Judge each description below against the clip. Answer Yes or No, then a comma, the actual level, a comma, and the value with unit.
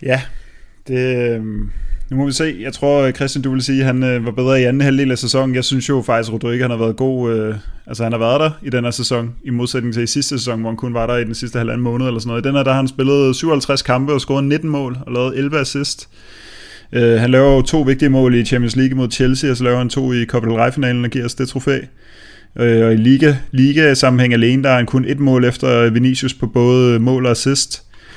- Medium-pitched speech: No, low, 125 Hz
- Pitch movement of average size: No, narrow, 2.1 semitones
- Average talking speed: No, fast, 265 wpm